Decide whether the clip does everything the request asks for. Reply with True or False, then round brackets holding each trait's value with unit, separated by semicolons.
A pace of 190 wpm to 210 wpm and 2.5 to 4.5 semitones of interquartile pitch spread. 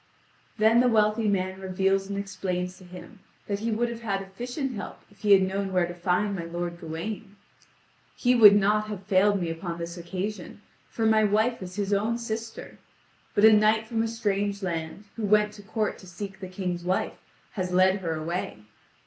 True (195 wpm; 2.8 semitones)